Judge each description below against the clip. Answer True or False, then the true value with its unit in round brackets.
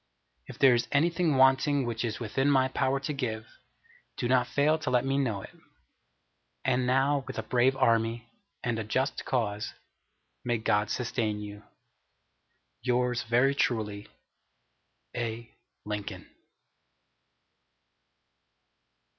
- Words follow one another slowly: True (120 wpm)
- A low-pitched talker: True (125 Hz)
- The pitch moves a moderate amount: True (3.0 semitones)